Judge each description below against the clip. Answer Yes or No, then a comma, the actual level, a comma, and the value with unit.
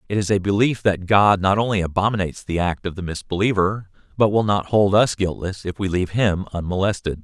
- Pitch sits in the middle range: No, low, 100 Hz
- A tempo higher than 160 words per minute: Yes, fast, 205 wpm